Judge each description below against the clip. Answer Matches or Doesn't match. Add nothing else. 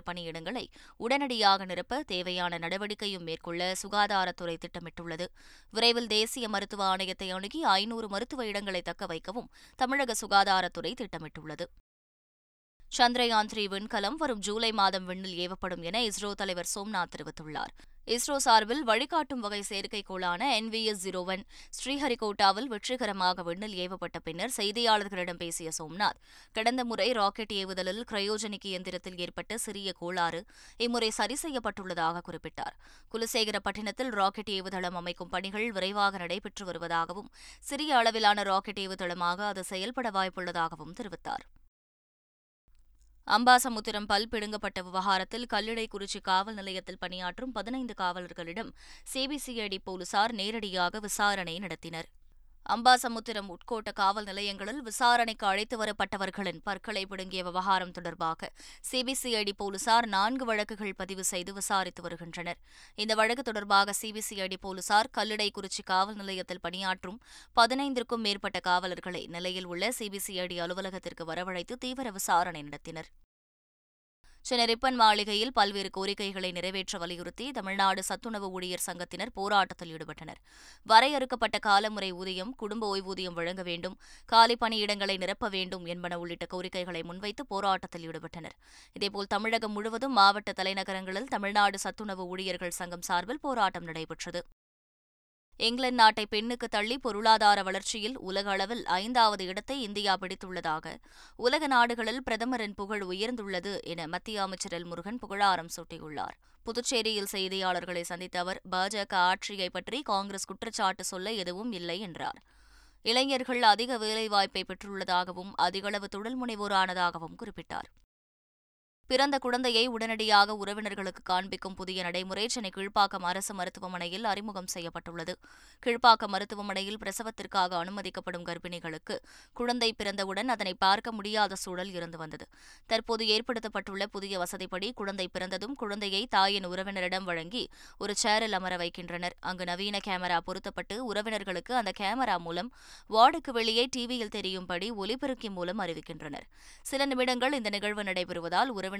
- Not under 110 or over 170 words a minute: Matches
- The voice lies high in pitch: Matches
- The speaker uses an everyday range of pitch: Matches